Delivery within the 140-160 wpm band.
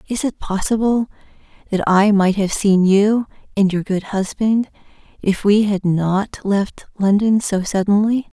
Yes: average, 150 wpm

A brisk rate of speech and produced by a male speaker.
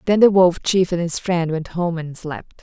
No: fast, 250 wpm; female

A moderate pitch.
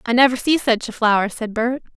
No: high, 235 Hz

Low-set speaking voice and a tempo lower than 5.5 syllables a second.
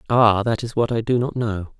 Yes: low, 115 Hz; 5.3 syllables/s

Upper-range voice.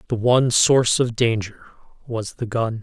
No: low, 115 Hz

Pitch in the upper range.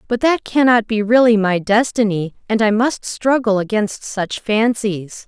Yes: high, 220 Hz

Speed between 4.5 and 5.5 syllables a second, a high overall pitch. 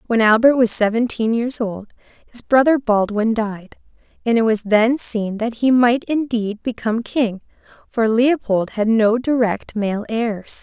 No: 4.2 syllables/s; high, 225 Hz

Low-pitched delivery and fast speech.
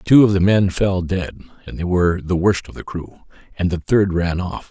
Yes: very low, 90 Hz; fast, 240 wpm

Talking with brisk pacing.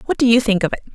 Yes: fast, 380 wpm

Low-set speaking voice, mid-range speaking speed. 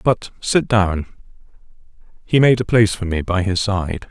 Yes: low, 100 Hz; average, 175 wpm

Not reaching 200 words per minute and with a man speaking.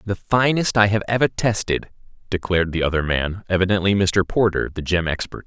Yes: average, 175 wpm; male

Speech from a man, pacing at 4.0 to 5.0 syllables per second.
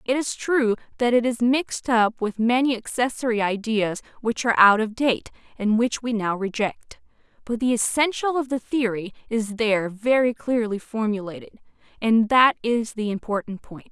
No: female; 4.9 syllables/s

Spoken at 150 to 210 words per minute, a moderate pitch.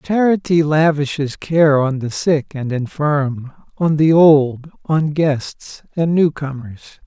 No: slow, 135 wpm; medium, 150 Hz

